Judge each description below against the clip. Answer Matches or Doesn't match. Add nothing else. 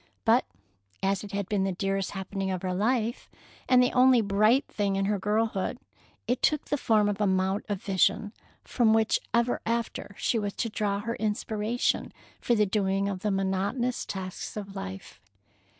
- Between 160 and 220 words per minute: Matches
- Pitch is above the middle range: Matches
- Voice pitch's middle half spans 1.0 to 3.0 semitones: Matches